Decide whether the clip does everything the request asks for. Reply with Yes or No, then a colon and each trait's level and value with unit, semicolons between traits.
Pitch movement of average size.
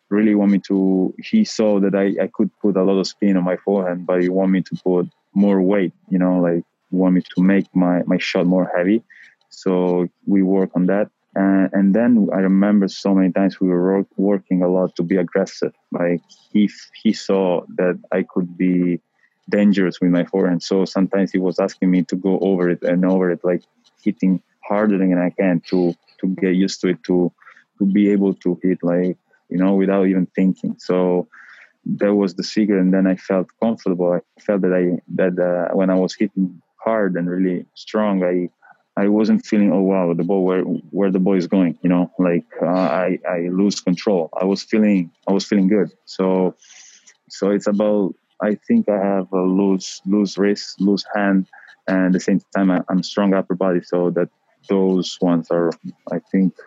No: narrow, 1.6 semitones